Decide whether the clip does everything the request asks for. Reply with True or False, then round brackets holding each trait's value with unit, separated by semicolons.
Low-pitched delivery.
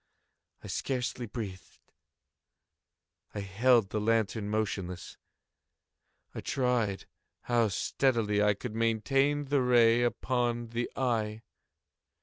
True (115 Hz)